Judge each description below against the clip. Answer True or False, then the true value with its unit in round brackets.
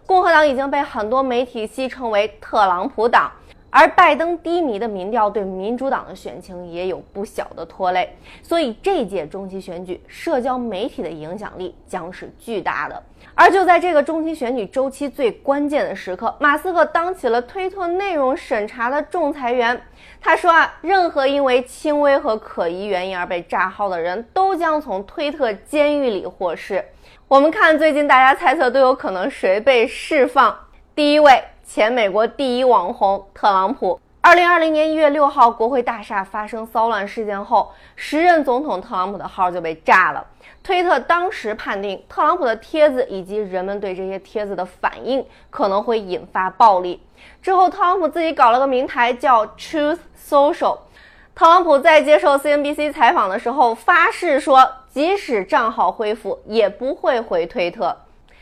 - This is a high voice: True (260 Hz)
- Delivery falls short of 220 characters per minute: False (280 characters per minute)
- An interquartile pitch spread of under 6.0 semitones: False (6.6 semitones)